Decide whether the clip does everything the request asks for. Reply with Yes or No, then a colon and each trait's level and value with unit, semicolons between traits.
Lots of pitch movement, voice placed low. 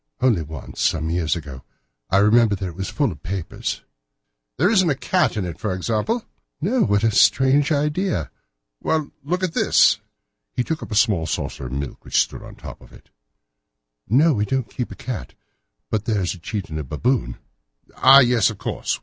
Yes: wide, 8.0 semitones; low, 110 Hz